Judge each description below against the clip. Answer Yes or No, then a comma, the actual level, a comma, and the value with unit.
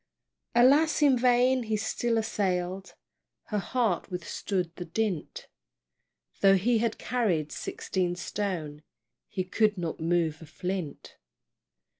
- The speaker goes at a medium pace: No, slow, 115 wpm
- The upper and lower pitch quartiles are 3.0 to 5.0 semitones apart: Yes, average, 4.7 semitones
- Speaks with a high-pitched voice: Yes, high, 195 Hz